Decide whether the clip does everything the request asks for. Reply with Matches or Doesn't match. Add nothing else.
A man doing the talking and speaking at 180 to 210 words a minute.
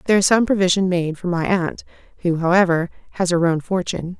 Doesn't match